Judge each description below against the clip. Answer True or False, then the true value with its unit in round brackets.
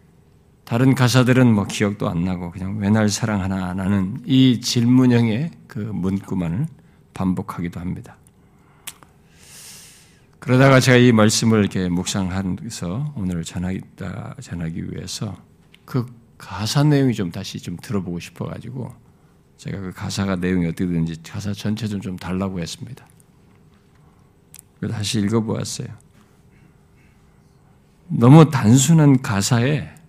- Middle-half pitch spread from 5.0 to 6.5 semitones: True (5.3 semitones)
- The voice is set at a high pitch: False (105 Hz)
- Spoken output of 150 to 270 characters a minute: True (265 characters per minute)